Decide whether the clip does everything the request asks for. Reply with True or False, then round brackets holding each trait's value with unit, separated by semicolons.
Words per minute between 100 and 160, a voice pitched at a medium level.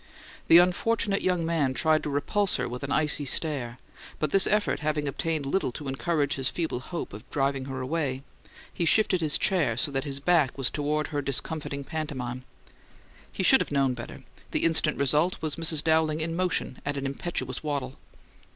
False (185 wpm; 150 Hz)